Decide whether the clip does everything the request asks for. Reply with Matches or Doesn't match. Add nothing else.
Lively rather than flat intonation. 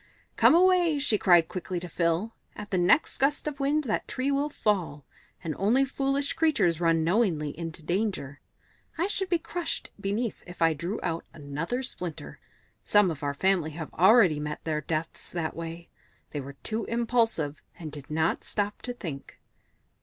Matches